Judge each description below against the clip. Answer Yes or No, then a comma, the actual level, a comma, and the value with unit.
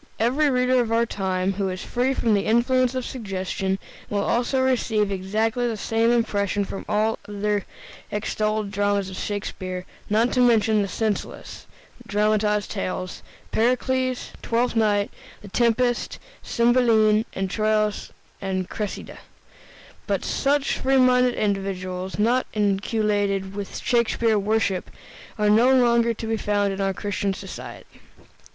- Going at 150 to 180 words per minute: No, slow, 135 wpm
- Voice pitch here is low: No, high, 215 Hz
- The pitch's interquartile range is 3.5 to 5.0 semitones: No, average, 3.0 semitones